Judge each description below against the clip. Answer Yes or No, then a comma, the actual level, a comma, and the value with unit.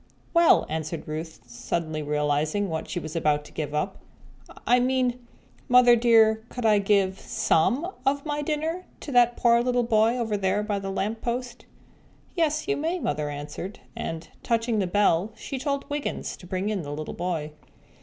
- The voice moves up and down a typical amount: No, wide, 7.5 semitones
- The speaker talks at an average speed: Yes, average, 175 wpm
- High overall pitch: Yes, high, 210 Hz